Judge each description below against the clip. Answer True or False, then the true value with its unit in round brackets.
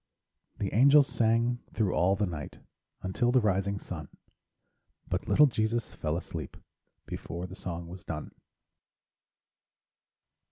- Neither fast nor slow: False (120 wpm)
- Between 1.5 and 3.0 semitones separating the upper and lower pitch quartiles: False (5.1 semitones)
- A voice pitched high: False (100 Hz)